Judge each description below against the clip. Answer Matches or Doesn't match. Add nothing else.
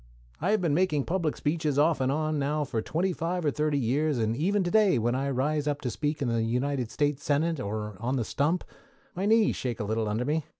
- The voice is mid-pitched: Matches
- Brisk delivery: Matches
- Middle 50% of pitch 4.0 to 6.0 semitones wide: Matches